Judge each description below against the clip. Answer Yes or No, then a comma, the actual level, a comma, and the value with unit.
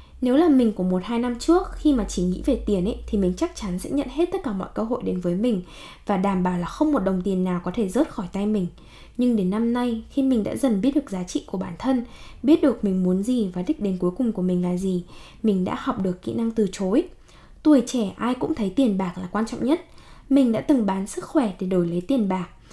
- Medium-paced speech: No, fast, 275 wpm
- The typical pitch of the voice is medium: No, high, 220 Hz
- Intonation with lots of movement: Yes, wide, 5.8 semitones